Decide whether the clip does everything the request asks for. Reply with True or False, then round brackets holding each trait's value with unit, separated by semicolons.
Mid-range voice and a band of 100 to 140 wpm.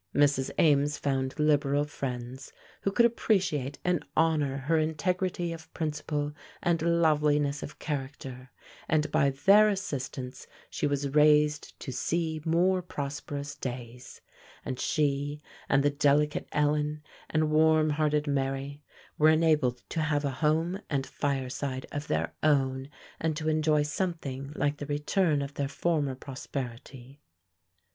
True (150 Hz; 135 wpm)